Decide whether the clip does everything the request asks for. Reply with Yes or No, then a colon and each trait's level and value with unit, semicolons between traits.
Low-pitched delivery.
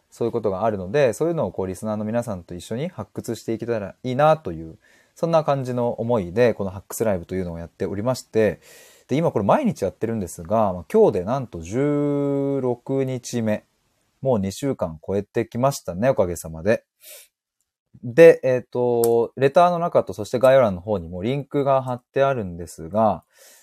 Yes: low, 115 Hz